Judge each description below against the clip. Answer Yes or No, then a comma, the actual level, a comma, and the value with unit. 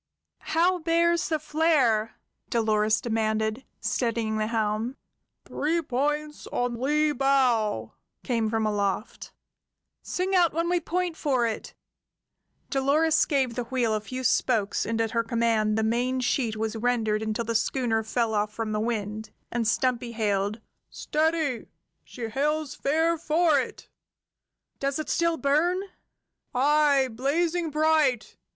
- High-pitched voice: Yes, high, 245 Hz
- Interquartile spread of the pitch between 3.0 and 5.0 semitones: No, wide, 5.5 semitones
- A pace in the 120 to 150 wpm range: Yes, slow, 135 wpm